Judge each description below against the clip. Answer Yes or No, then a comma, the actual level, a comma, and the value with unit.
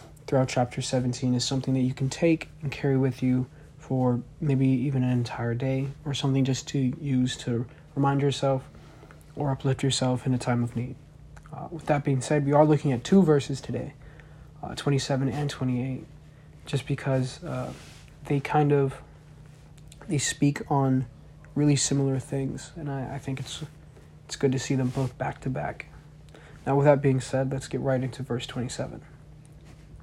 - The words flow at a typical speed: Yes, average, 175 wpm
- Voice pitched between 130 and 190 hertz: Yes, low, 135 Hz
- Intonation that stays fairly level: Yes, narrow, 2.1 semitones